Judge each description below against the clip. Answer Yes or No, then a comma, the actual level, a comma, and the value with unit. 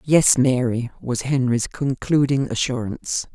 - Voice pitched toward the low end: Yes, low, 130 Hz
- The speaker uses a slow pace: Yes, slow, 110 wpm